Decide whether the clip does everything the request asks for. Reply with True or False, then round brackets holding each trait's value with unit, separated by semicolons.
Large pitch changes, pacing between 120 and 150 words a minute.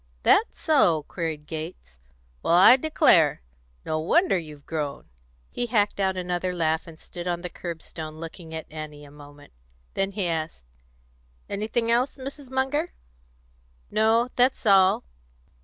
True (6.5 semitones; 140 wpm)